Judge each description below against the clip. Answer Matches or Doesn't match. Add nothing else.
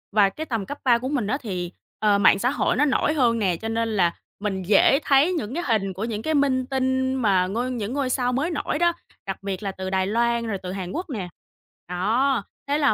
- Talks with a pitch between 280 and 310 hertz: Doesn't match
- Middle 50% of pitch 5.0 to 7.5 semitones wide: Matches